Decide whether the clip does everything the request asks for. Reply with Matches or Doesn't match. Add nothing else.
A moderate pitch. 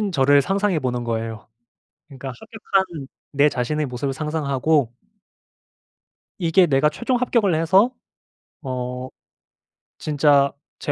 Matches